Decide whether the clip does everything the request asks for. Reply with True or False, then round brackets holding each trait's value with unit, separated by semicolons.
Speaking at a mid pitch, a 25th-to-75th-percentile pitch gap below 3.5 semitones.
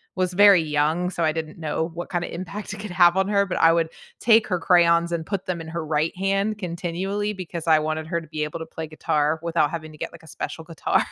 True (170 Hz; 2.7 semitones)